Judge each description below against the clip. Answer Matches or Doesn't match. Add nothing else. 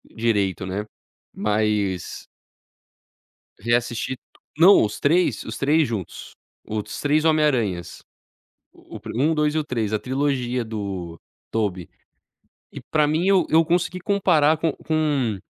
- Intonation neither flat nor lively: Doesn't match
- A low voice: Matches